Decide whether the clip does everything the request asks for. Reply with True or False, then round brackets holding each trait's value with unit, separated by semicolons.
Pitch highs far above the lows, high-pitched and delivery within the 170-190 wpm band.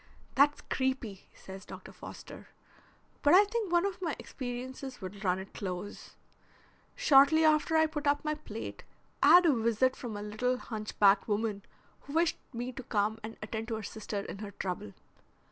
True (6.2 semitones; 245 Hz; 180 wpm)